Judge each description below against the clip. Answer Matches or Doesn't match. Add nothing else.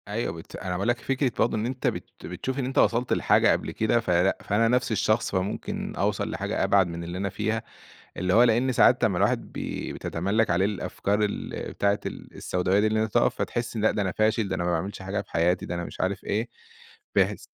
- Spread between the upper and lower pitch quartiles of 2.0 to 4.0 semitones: Matches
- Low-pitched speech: Matches